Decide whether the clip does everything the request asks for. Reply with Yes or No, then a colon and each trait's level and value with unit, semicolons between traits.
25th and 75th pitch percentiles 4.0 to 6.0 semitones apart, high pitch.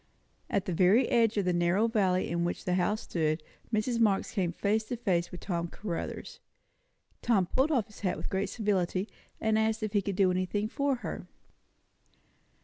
No: average, 3.4 semitones; high, 200 Hz